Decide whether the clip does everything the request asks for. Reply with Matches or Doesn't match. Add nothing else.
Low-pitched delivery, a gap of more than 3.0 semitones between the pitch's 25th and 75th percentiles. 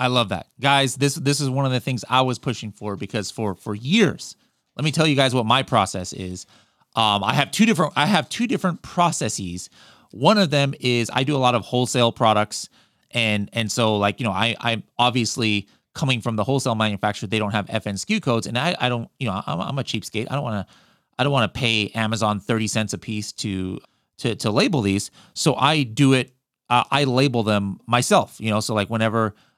Matches